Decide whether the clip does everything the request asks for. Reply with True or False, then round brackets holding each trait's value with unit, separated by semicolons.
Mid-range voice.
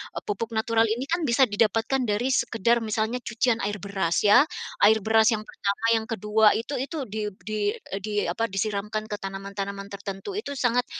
False (220 Hz)